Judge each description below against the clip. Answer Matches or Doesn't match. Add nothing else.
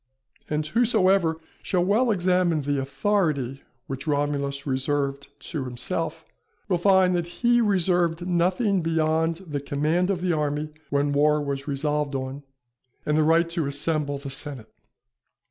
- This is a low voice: Doesn't match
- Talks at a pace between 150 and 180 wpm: Doesn't match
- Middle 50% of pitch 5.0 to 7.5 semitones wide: Doesn't match